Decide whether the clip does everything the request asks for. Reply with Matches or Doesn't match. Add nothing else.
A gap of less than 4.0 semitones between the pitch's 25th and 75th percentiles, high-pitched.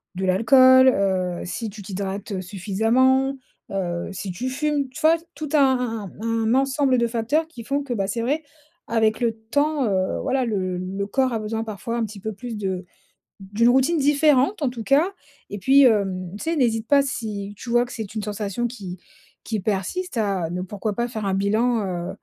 Doesn't match